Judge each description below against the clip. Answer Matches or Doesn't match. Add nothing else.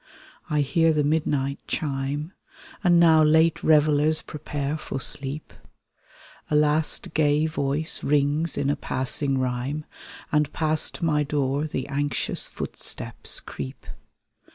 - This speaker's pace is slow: Matches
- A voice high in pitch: Doesn't match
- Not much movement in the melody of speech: Matches